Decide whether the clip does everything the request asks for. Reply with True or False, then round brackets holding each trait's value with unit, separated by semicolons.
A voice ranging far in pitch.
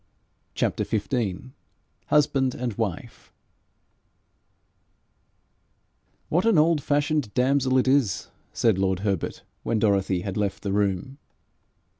True (5.9 semitones)